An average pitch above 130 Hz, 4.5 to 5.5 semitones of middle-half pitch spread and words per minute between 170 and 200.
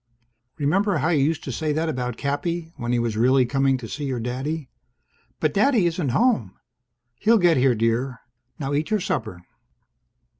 Yes: medium, 140 Hz; average, 4.8 semitones; average, 175 wpm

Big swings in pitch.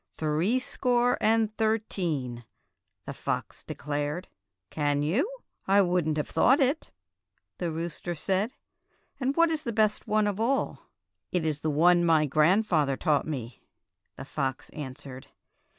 Yes: wide, 6.7 semitones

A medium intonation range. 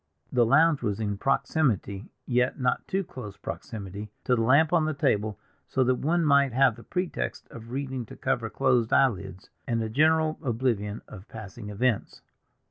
Yes: average, 4.4 semitones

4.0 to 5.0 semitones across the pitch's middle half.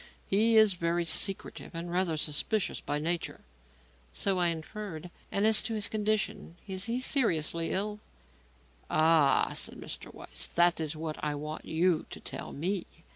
Yes: average, 4.4 semitones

